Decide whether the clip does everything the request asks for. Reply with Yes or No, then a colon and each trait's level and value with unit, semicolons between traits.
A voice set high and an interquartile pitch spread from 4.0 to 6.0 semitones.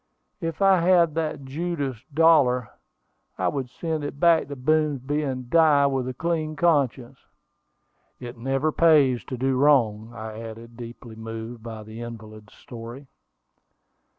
No: low, 135 Hz; average, 4.8 semitones